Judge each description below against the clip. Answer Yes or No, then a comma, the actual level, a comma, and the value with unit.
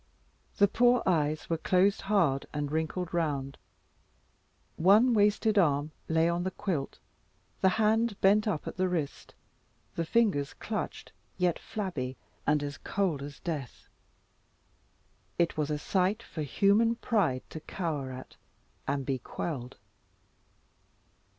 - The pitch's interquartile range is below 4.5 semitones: No, wide, 5.5 semitones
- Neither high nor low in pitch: Yes, medium, 170 Hz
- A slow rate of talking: Yes, slow, 130 wpm